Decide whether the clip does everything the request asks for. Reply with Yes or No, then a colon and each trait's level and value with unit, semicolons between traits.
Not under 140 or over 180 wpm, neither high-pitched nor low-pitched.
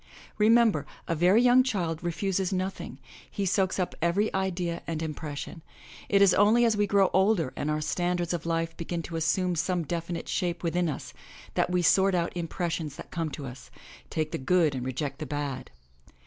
No: average, 195 wpm; medium, 175 Hz